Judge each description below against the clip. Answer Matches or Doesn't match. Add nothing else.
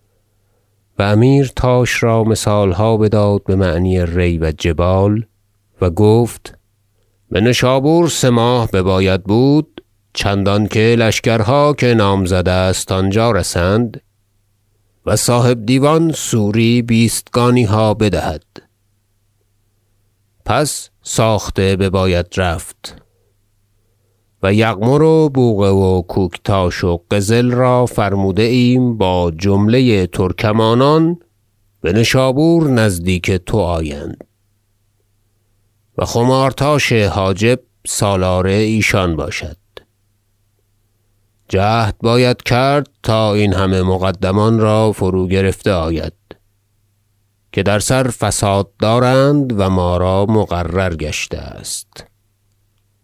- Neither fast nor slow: Doesn't match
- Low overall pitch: Matches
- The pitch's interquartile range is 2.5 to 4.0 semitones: Matches